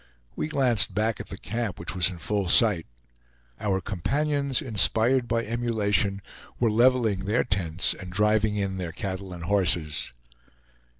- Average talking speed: Yes, average, 145 wpm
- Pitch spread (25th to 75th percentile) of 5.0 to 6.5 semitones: No, average, 3.8 semitones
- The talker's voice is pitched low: Yes, low, 105 Hz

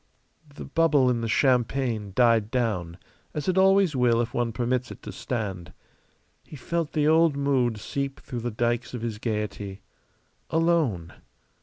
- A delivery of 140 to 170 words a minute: Yes, average, 155 wpm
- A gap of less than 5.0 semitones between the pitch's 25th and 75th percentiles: Yes, average, 4.2 semitones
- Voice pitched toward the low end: Yes, low, 120 Hz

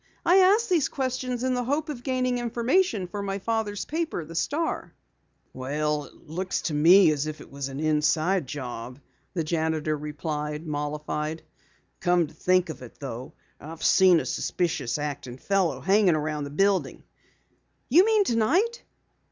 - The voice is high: No, medium, 170 Hz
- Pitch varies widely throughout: Yes, wide, 8.2 semitones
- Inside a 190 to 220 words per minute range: No, average, 160 wpm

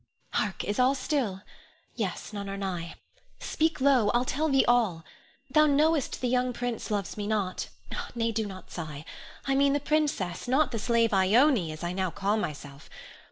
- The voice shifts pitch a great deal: Yes, wide, 6.0 semitones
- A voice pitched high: Yes, high, 225 Hz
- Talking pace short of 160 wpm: No, average, 175 wpm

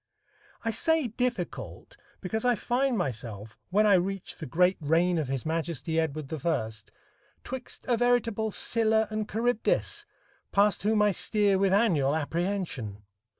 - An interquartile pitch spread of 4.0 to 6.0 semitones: Yes, wide, 5.6 semitones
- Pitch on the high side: Yes, high, 195 Hz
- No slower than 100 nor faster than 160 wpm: Yes, average, 140 wpm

